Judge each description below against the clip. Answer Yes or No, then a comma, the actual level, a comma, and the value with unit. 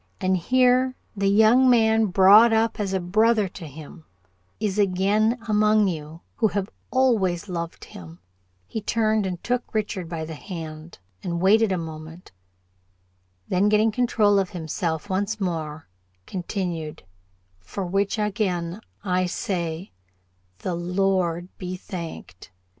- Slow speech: Yes, slow, 130 wpm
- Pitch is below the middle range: No, high, 190 Hz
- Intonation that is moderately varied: Yes, average, 4.0 semitones